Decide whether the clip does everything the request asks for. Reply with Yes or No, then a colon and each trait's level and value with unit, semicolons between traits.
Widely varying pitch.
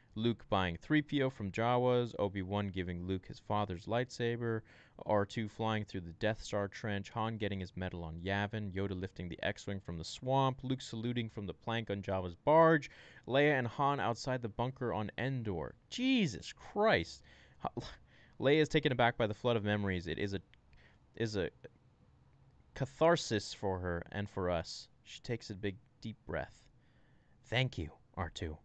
No: average, 4.5 semitones